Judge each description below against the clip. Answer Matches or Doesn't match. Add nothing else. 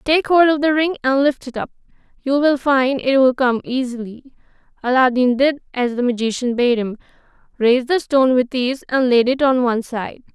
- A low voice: Doesn't match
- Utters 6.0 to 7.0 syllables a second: Doesn't match